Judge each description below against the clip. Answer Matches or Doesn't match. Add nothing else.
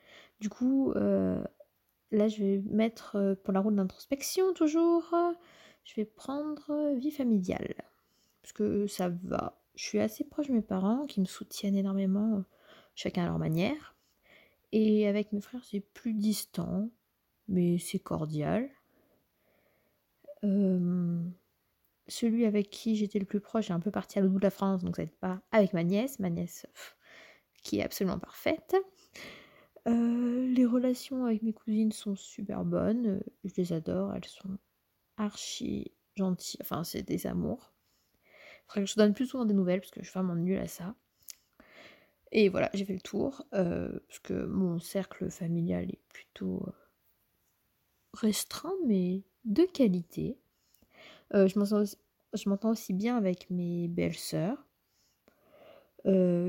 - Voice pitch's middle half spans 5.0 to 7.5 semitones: Doesn't match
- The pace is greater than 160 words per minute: Doesn't match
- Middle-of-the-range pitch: Doesn't match